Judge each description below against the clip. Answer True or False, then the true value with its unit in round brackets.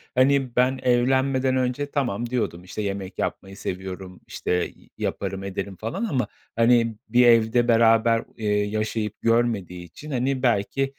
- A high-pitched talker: False (115 Hz)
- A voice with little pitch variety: False (4.1 semitones)